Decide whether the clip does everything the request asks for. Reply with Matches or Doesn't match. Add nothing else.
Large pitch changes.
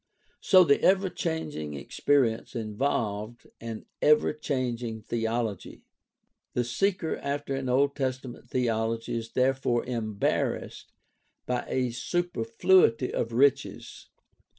Doesn't match